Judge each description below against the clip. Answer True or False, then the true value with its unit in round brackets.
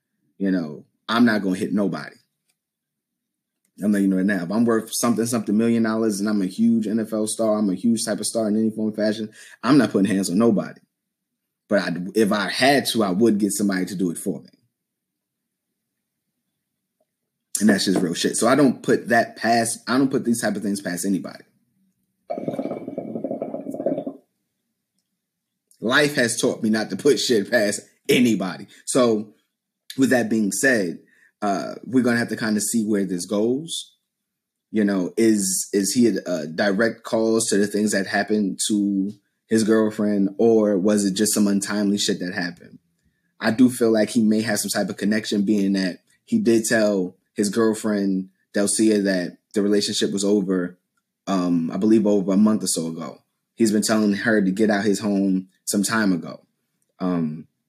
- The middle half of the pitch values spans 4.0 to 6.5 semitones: False (2.6 semitones)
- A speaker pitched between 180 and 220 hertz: False (105 Hz)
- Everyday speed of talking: True (185 wpm)